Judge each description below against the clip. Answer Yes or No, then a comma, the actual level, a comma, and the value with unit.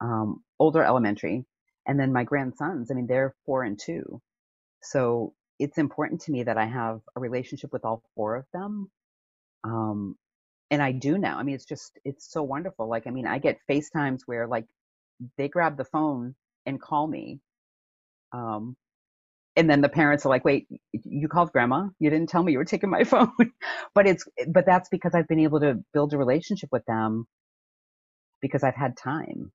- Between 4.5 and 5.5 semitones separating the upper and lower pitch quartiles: Yes, average, 5.0 semitones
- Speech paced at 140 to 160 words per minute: No, average, 190 wpm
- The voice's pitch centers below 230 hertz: Yes, medium, 140 Hz